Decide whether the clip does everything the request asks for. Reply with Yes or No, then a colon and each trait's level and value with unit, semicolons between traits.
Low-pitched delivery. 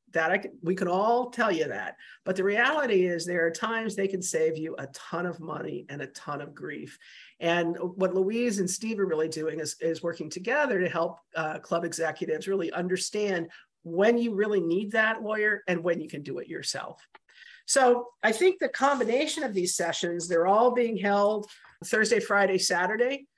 No: high, 190 Hz